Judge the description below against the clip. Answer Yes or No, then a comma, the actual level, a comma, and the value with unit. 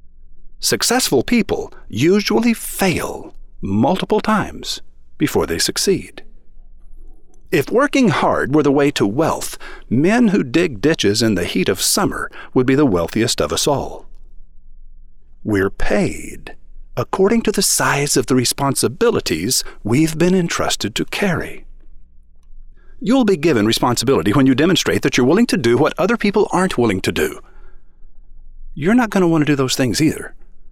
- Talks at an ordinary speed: Yes, average, 150 wpm